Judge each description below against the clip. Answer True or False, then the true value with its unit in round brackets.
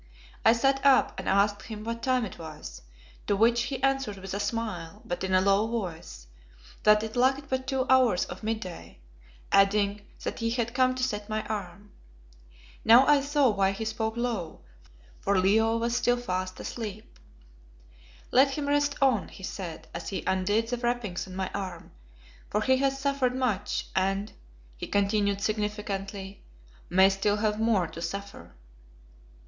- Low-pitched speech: False (215 Hz)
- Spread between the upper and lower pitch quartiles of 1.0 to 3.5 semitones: False (3.9 semitones)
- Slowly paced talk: False (165 wpm)